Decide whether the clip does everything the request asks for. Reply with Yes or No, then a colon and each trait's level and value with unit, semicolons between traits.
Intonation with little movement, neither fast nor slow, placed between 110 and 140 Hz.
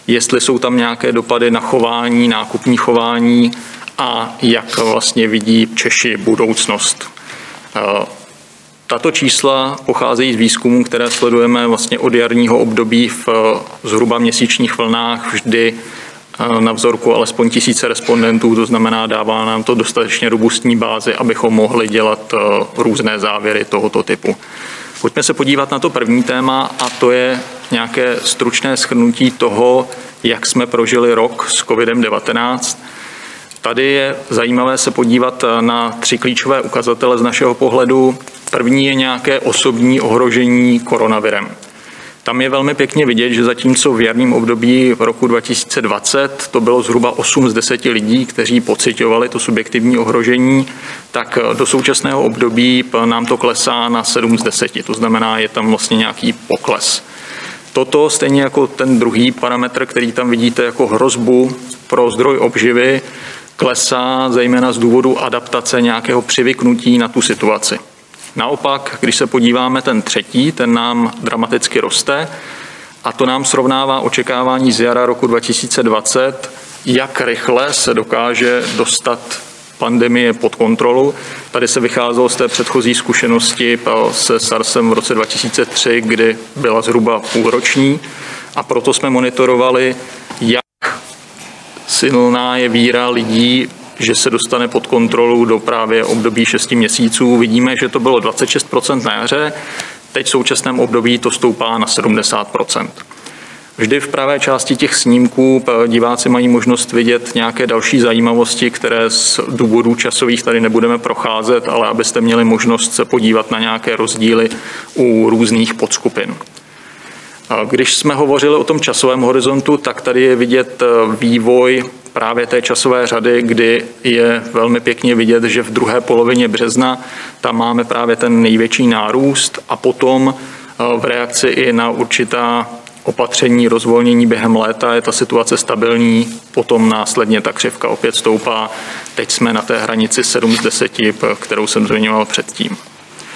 Yes: narrow, 1.6 semitones; average, 140 wpm; low, 120 Hz